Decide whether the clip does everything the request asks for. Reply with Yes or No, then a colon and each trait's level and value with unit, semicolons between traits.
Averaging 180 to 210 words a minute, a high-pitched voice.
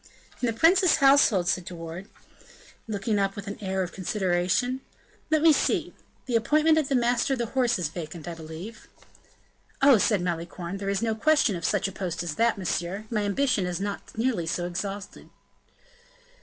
Yes: average, 185 wpm; high, 200 Hz